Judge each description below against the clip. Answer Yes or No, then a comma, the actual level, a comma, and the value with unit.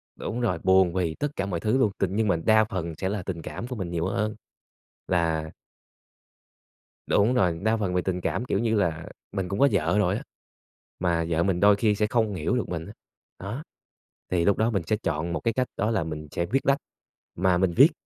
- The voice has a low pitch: Yes, very low, 95 Hz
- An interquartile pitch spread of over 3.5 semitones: Yes, average, 4.3 semitones